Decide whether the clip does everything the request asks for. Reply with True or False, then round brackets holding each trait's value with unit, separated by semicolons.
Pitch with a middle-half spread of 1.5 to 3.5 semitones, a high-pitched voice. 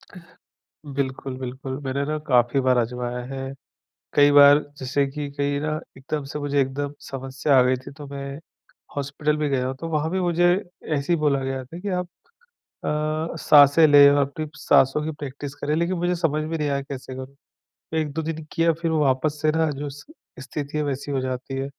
False (2.4 semitones; 145 Hz)